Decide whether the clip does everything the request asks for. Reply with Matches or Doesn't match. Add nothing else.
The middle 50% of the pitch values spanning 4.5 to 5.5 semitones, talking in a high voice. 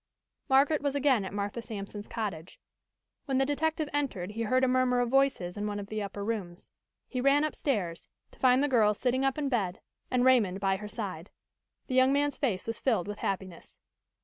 Matches